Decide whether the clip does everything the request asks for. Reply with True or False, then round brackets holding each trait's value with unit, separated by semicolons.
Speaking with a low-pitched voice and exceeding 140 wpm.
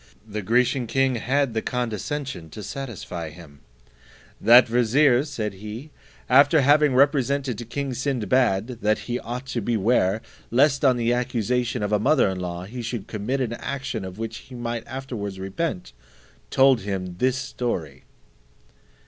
True (120 Hz; 150 wpm)